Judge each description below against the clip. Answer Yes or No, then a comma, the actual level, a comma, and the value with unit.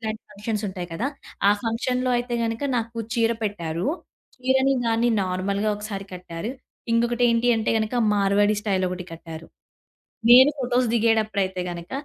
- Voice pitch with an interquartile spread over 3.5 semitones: Yes, average, 3.9 semitones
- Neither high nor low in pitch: No, high, 215 Hz